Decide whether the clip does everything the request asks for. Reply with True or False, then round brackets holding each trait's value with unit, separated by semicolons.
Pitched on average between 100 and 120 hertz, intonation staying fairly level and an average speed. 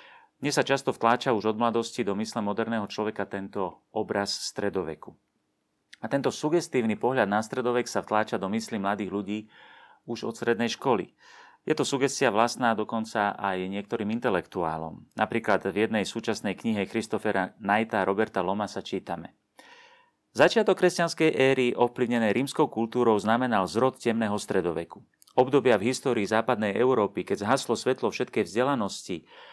False (115 Hz; 3.5 semitones; 140 wpm)